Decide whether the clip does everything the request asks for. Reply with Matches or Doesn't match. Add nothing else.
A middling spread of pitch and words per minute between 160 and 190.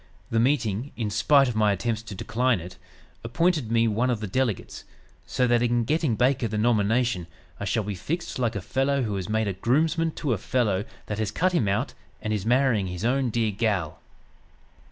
Doesn't match